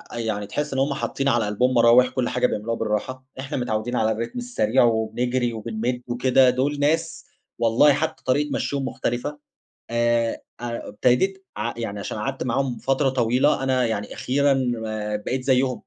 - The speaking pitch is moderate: No, low, 125 Hz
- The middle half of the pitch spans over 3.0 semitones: No, narrow, 2.6 semitones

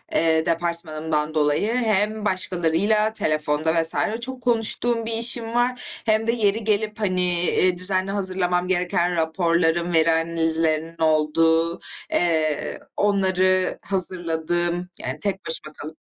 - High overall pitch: No, medium, 175 Hz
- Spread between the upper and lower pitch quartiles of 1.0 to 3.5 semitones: No, average, 4.1 semitones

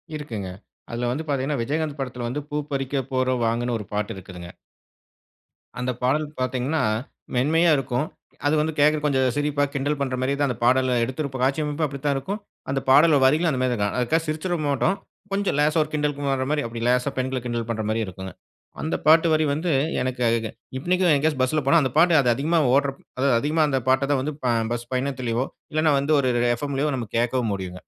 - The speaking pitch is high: No, low, 135 Hz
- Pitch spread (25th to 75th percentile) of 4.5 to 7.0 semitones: No, average, 3.3 semitones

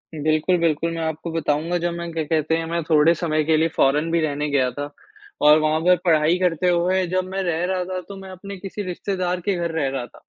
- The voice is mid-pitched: Yes, medium, 165 Hz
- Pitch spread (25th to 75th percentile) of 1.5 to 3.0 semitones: Yes, average, 2.7 semitones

